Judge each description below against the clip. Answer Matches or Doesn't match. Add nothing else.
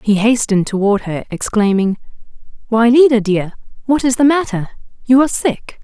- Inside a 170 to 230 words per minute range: Doesn't match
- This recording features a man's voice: Doesn't match